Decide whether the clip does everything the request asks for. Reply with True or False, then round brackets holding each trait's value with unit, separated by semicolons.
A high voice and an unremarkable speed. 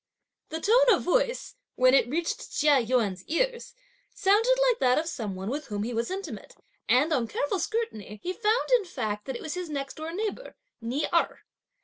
True (310 Hz; 195 wpm)